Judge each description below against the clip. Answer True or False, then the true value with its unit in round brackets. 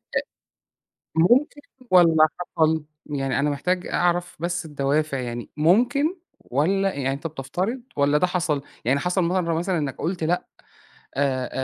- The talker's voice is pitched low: False (160 Hz)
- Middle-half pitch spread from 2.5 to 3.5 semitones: False (4.2 semitones)